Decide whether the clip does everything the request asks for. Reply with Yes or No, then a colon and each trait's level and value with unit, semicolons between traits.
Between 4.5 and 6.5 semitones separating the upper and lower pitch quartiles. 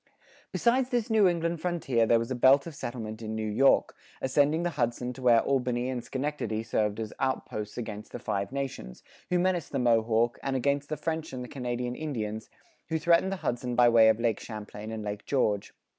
Yes: average, 5.0 semitones